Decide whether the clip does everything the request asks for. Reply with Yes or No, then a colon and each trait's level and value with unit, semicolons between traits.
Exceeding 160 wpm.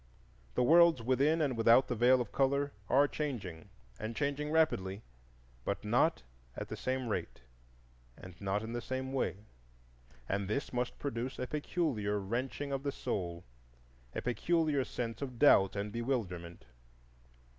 No: average, 145 wpm